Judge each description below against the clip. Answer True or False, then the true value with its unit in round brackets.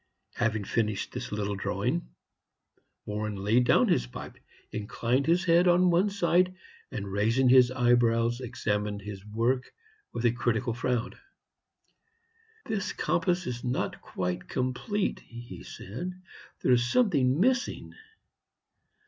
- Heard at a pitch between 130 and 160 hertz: False (120 Hz)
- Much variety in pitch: True (7.7 semitones)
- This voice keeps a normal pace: False (125 wpm)